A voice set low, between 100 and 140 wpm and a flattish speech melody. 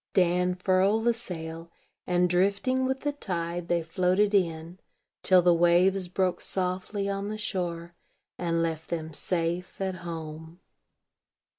No: medium, 180 Hz; slow, 135 wpm; narrow, 2.3 semitones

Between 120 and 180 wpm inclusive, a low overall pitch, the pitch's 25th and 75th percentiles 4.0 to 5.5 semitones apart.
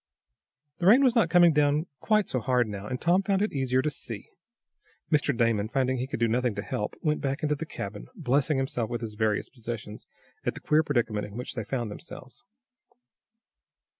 No: average, 195 wpm; low, 130 Hz; average, 4.9 semitones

